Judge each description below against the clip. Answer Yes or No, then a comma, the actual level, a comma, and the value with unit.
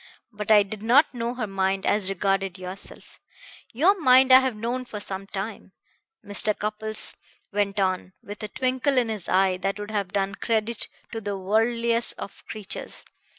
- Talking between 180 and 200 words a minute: No, average, 170 wpm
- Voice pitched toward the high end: Yes, high, 210 Hz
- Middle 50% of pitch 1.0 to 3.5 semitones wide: Yes, average, 3.1 semitones